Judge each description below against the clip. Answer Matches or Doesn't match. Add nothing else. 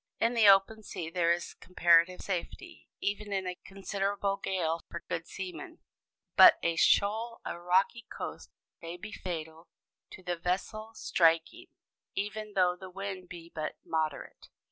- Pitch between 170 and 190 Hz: Matches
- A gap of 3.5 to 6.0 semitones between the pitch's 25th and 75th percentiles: Doesn't match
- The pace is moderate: Matches